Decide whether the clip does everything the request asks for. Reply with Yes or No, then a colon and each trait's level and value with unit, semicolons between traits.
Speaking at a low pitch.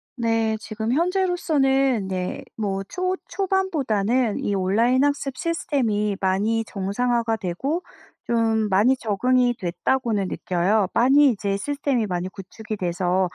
No: high, 225 Hz